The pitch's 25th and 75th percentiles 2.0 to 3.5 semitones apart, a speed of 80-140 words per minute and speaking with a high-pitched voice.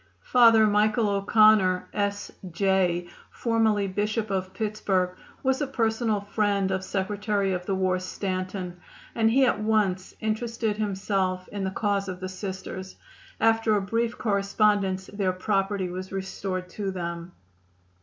Yes: narrow, 2.4 semitones; slow, 135 wpm; high, 200 Hz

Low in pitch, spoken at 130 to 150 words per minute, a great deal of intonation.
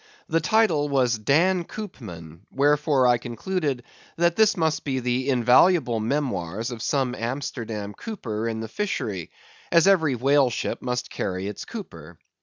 Yes: low, 130 Hz; average, 145 wpm; wide, 6.0 semitones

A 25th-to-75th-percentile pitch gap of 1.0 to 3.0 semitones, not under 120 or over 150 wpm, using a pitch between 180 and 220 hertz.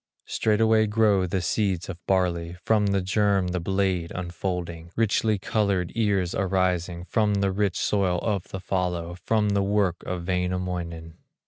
No: narrow, 2.5 semitones; average, 145 wpm; very low, 95 Hz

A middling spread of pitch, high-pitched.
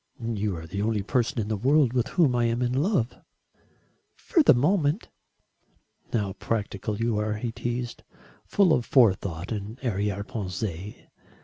No: average, 3.7 semitones; low, 115 Hz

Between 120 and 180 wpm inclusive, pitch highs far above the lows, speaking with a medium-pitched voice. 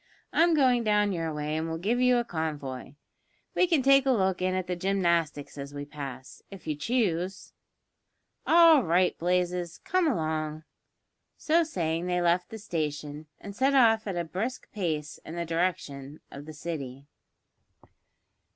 Yes: average, 160 wpm; wide, 6.2 semitones; medium, 175 Hz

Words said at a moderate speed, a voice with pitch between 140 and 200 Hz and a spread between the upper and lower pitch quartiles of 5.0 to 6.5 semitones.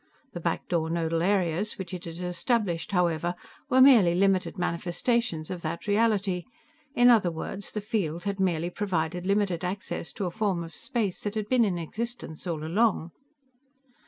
No: average, 165 wpm; medium, 185 Hz; average, 3.6 semitones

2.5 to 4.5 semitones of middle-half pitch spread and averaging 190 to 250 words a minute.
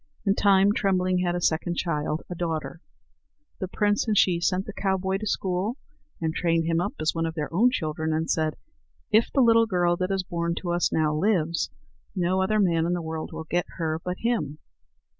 Yes: average, 3.0 semitones; fast, 205 wpm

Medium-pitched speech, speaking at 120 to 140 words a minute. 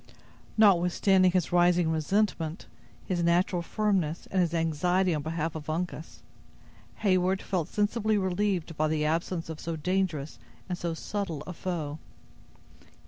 Yes: medium, 175 Hz; slow, 135 wpm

